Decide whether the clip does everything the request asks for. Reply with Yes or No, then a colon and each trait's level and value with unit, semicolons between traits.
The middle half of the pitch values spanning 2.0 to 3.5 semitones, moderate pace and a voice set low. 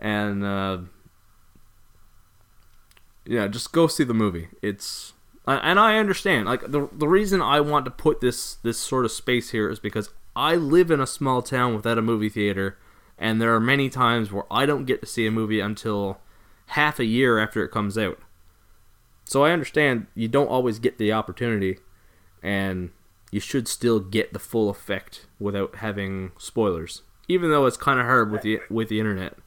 No: average, 4.4 semitones; average, 185 wpm; low, 110 Hz